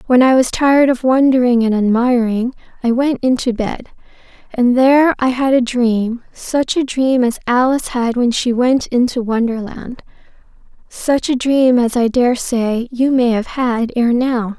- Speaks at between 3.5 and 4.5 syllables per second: Yes, 4.4 syllables/s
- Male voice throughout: No, female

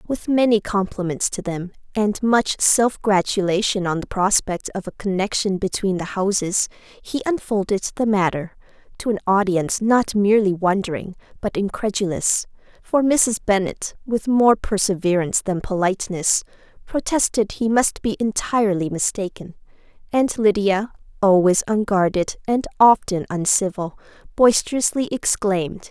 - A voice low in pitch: No, high, 205 Hz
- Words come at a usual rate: No, slow, 120 wpm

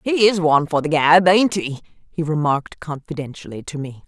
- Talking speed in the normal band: Yes, average, 190 wpm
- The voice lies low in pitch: No, medium, 160 Hz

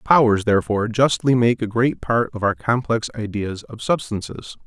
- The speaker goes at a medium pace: Yes, average, 165 wpm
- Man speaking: Yes, male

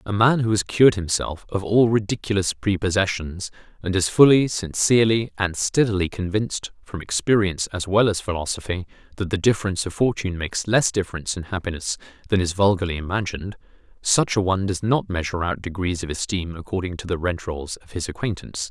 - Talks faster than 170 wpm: Yes, average, 180 wpm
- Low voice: Yes, very low, 95 Hz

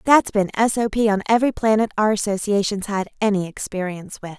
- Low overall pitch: No, high, 205 Hz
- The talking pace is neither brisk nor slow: Yes, average, 165 wpm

